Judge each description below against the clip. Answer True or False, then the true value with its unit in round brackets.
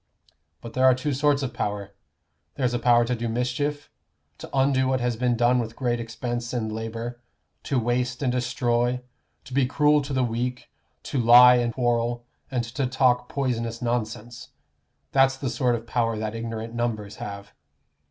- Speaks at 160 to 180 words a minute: True (170 wpm)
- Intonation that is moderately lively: False (1.8 semitones)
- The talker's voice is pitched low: True (120 Hz)